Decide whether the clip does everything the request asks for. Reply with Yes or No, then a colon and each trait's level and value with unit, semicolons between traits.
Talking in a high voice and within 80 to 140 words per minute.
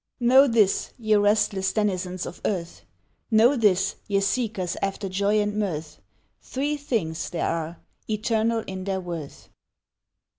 Yes: high, 205 Hz; slow, 135 wpm